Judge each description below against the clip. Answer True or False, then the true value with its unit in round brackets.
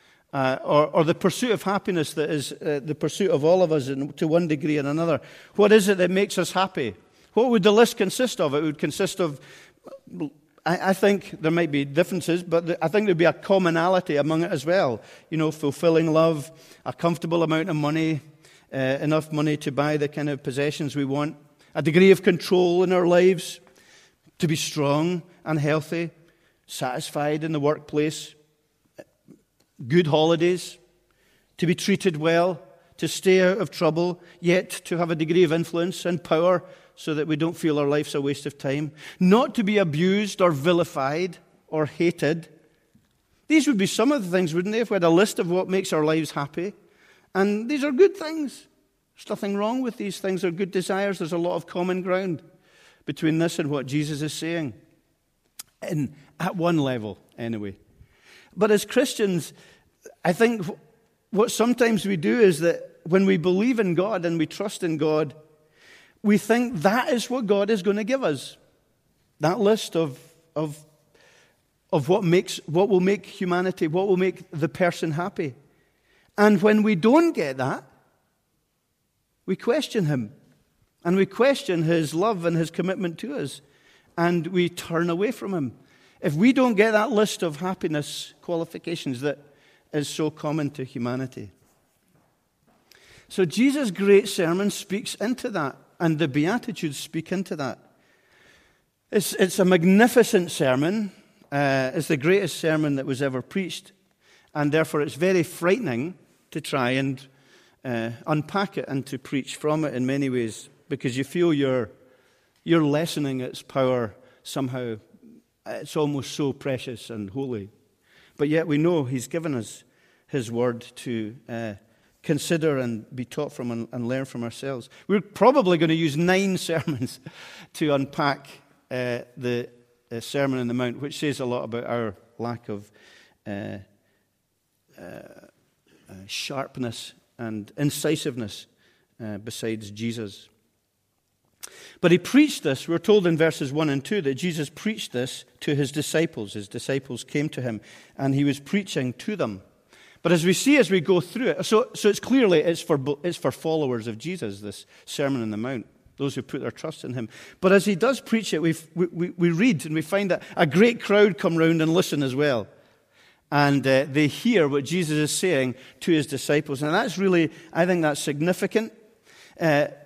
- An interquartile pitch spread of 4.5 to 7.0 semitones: True (4.8 semitones)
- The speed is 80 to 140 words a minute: False (175 wpm)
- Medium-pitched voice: True (160 Hz)